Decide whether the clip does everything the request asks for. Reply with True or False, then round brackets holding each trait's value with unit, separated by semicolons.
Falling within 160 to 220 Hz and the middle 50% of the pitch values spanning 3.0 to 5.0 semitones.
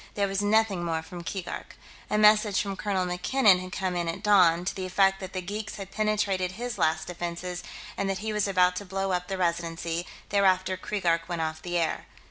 False (185 Hz; 2.5 semitones)